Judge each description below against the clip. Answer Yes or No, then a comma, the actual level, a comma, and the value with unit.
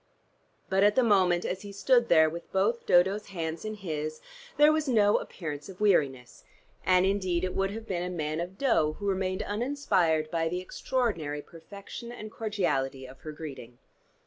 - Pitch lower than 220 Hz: Yes, medium, 185 Hz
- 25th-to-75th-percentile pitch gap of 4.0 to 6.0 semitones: Yes, average, 4.7 semitones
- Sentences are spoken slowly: No, average, 175 wpm